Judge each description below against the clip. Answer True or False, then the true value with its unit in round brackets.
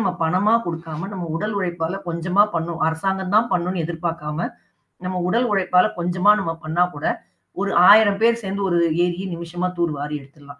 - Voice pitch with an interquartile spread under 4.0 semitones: True (2.8 semitones)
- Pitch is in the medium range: True (175 Hz)